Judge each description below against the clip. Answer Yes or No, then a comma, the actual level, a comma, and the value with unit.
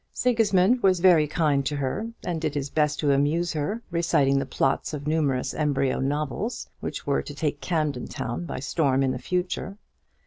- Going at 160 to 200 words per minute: Yes, average, 180 wpm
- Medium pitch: Yes, medium, 150 Hz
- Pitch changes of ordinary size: Yes, average, 3.9 semitones